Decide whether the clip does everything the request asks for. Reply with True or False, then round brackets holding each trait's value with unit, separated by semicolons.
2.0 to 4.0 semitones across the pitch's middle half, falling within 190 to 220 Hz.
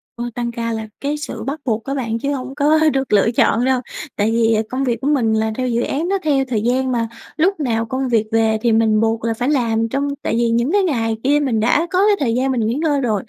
False (3.6 semitones; 245 Hz)